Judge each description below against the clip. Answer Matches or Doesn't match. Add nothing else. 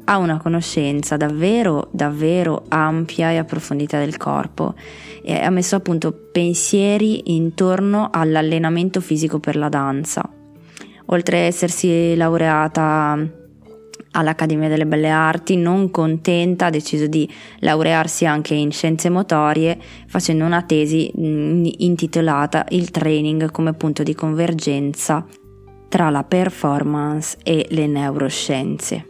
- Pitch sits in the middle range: Matches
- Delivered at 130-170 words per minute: Doesn't match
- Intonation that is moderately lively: Doesn't match